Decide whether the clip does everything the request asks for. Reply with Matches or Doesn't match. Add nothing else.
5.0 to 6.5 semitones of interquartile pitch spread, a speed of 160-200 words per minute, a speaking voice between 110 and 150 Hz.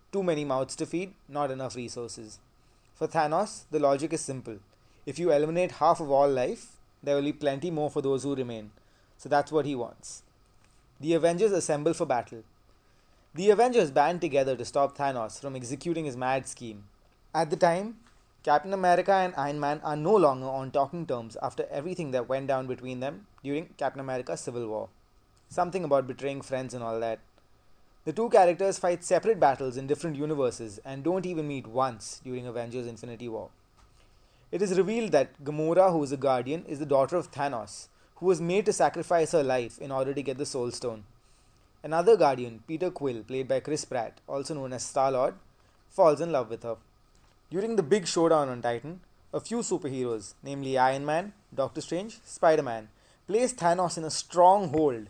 Matches